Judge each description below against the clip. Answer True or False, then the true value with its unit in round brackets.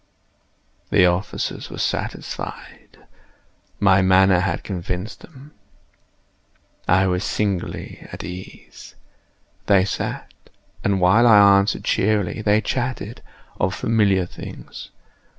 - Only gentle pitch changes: True (2.3 semitones)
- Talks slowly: True (100 wpm)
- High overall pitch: False (95 Hz)